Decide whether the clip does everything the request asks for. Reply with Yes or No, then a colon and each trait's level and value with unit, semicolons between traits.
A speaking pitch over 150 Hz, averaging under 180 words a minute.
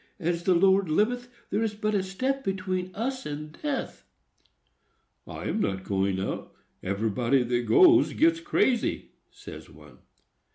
Yes: high, 190 Hz; average, 140 wpm